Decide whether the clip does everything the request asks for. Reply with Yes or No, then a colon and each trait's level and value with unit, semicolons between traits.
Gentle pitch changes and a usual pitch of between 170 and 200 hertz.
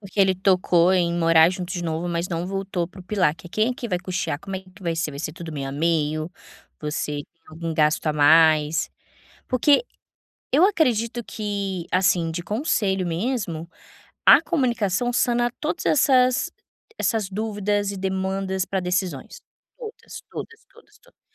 No: average, 4.3 semitones; medium, 185 Hz